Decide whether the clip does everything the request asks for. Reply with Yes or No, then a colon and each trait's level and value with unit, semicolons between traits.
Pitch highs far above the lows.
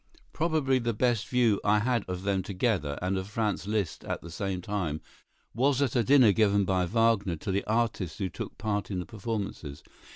No: average, 3.8 semitones